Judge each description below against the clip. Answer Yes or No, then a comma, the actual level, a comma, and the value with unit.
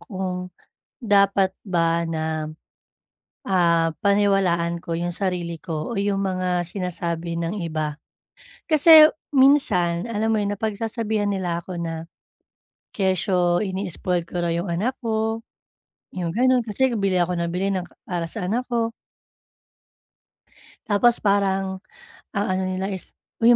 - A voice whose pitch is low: No, high, 190 Hz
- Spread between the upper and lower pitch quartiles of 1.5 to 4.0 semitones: Yes, average, 3.4 semitones